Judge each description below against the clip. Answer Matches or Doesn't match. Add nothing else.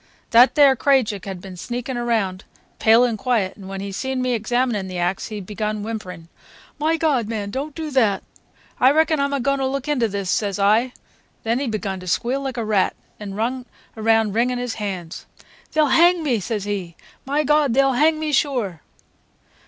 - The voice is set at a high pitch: Matches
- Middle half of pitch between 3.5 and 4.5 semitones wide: Doesn't match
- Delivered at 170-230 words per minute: Matches